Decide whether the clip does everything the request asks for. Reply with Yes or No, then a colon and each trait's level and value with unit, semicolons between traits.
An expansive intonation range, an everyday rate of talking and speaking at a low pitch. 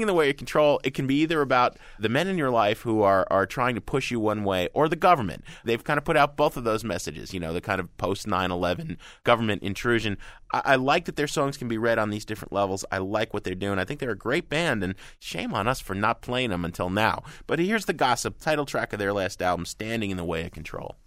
No: wide, 6.2 semitones; fast, 275 wpm; low, 110 Hz